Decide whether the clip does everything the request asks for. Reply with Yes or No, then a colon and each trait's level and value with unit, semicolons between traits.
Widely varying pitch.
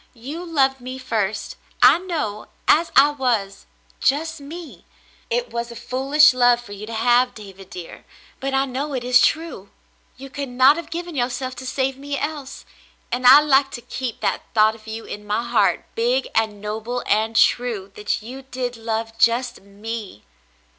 No: average, 3.9 semitones